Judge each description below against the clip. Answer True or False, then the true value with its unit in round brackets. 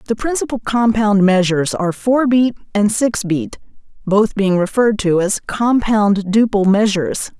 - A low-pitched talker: False (210 Hz)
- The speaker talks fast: False (145 wpm)